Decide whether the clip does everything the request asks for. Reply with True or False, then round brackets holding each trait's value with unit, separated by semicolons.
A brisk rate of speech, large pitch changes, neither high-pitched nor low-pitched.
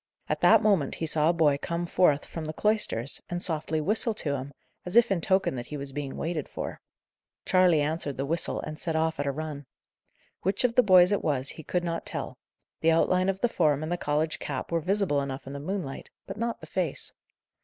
False (225 wpm; 4.1 semitones; 160 Hz)